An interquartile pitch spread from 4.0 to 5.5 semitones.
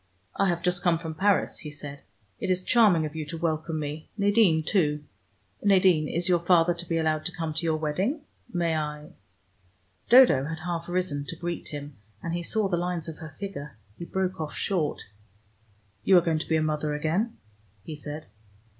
No: average, 2.8 semitones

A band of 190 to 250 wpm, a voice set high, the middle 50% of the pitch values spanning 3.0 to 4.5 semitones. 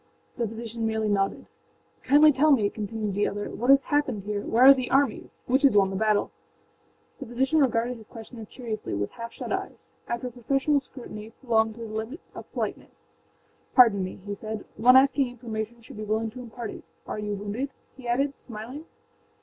Yes: average, 195 wpm; high, 230 Hz; average, 3.3 semitones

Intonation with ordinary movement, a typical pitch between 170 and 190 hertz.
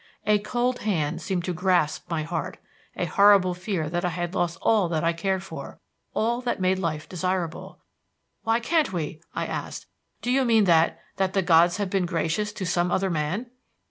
Yes: average, 3.4 semitones; medium, 185 Hz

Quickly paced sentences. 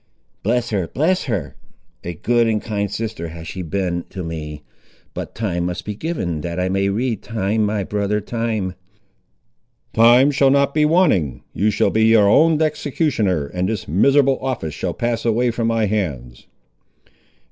No: average, 165 wpm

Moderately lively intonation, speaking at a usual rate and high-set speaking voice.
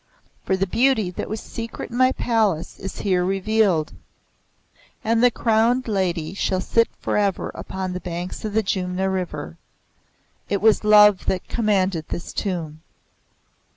Yes: average, 3.3 semitones; average, 145 wpm; high, 195 Hz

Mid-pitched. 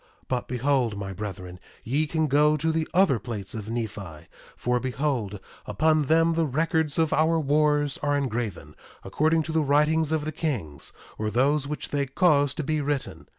Yes: medium, 145 Hz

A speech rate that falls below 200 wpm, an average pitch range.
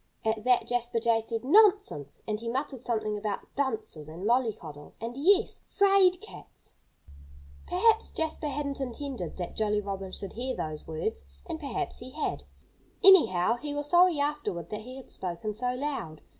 No: average, 160 wpm; wide, 5.9 semitones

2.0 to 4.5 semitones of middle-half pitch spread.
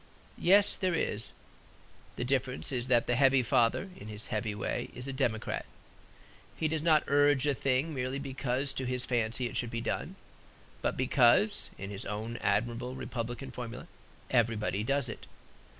Yes: average, 2.9 semitones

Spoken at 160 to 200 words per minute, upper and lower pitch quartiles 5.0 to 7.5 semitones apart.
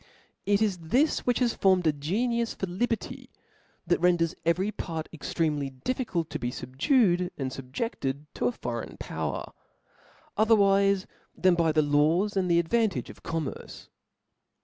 No: average, 145 wpm; average, 5.3 semitones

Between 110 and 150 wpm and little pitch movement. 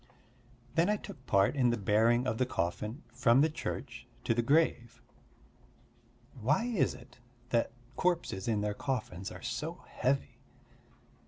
No: average, 145 wpm; average, 4.4 semitones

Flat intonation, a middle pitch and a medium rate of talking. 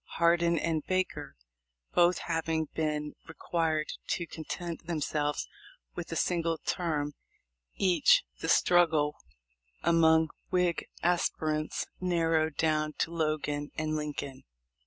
No: narrow, 1.9 semitones; medium, 160 Hz; slow, 105 wpm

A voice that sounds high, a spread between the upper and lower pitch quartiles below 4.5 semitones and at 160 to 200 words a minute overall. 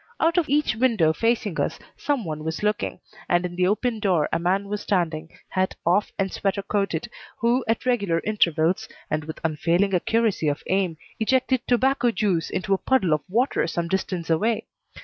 No: high, 195 Hz; average, 5.2 semitones; average, 180 wpm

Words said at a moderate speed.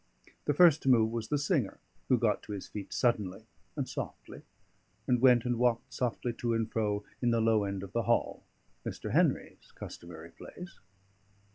Yes: average, 175 wpm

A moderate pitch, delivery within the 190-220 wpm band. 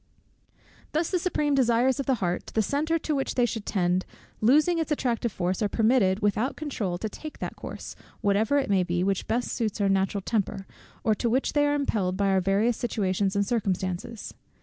No: high, 220 Hz; average, 195 wpm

